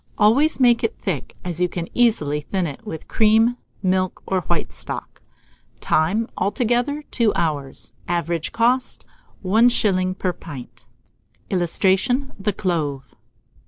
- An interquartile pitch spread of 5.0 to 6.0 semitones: Yes, average, 5.3 semitones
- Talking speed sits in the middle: No, slow, 125 wpm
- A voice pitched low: No, high, 190 Hz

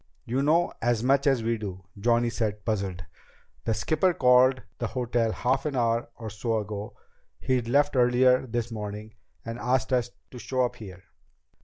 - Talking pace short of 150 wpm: No, average, 170 wpm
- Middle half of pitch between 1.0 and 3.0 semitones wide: Yes, average, 2.7 semitones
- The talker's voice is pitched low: Yes, low, 120 Hz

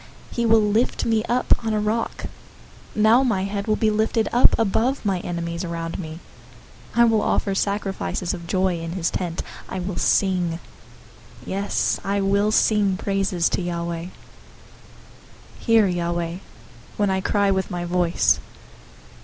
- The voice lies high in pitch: Yes, high, 195 Hz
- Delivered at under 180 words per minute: Yes, average, 155 wpm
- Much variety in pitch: No, average, 3.5 semitones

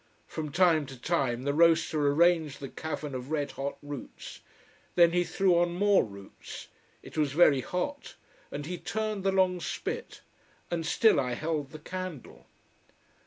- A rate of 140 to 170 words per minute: Yes, average, 160 wpm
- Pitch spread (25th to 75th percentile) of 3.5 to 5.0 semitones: Yes, average, 3.9 semitones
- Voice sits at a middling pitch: Yes, medium, 160 Hz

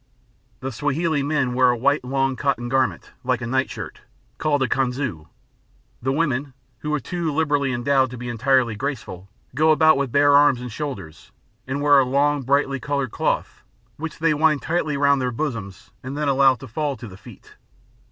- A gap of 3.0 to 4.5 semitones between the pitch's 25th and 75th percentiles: No, narrow, 2.6 semitones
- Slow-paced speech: No, average, 185 wpm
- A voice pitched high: No, low, 135 Hz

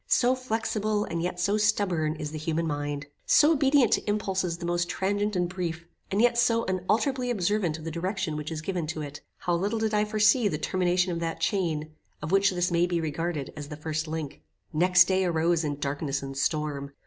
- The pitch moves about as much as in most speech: Yes, average, 4.7 semitones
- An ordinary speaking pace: No, fast, 210 wpm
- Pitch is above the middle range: No, medium, 175 Hz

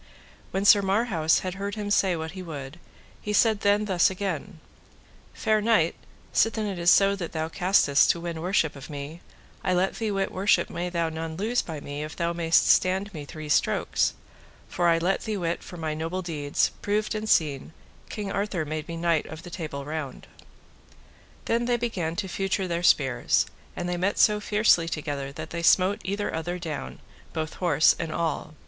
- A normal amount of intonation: Yes, average, 3.9 semitones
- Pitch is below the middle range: No, medium, 175 Hz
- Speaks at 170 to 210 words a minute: Yes, average, 190 wpm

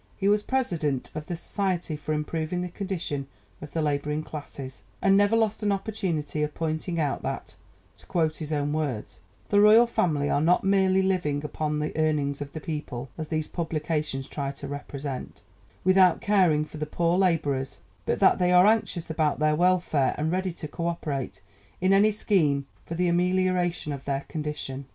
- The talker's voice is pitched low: No, medium, 160 Hz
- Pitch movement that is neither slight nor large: Yes, average, 3.8 semitones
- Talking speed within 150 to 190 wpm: Yes, average, 180 wpm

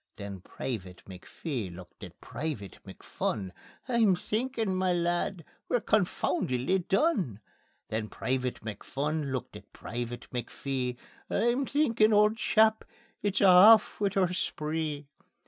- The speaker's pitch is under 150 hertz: No, medium, 165 Hz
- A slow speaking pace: Yes, slow, 120 wpm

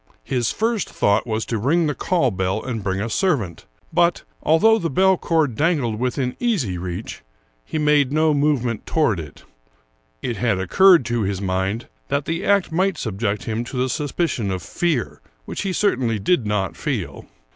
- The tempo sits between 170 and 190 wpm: Yes, average, 175 wpm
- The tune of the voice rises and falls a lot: Yes, wide, 7.5 semitones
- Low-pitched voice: Yes, low, 125 Hz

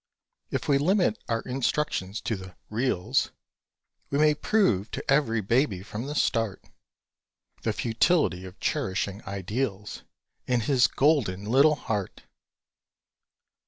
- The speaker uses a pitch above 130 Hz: No, low, 115 Hz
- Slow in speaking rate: Yes, slow, 120 wpm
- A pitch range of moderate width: No, wide, 6.2 semitones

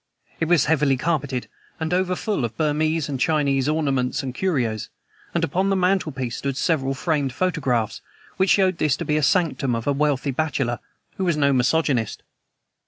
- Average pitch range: Yes, average, 3.9 semitones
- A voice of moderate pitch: Yes, medium, 150 Hz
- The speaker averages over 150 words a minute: Yes, average, 170 wpm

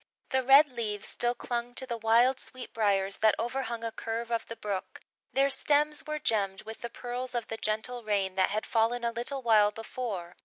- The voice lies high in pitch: Yes, high, 230 Hz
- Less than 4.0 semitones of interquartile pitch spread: Yes, narrow, 2.6 semitones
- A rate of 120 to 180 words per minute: No, average, 200 wpm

